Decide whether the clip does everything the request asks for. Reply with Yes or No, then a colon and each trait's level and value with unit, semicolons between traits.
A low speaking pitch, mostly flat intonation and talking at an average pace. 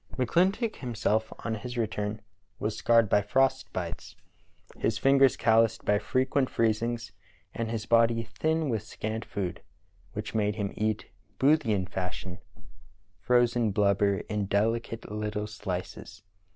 No: low, 110 Hz; narrow, 2.3 semitones; slow, 125 wpm